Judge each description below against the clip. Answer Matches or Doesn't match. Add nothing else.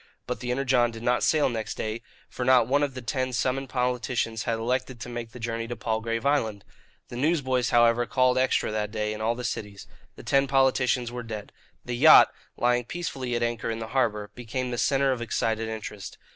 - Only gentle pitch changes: Matches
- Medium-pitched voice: Doesn't match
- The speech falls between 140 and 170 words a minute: Doesn't match